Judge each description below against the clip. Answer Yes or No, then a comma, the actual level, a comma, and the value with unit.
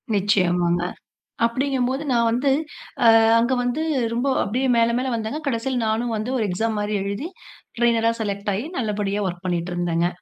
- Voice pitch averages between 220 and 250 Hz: Yes, high, 225 Hz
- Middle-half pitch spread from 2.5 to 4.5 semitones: Yes, average, 3.7 semitones